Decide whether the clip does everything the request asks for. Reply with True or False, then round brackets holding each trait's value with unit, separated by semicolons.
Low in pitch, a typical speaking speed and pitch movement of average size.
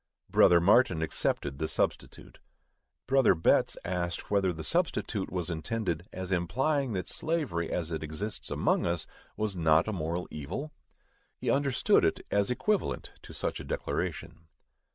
False (90 Hz; 145 wpm; 5.7 semitones)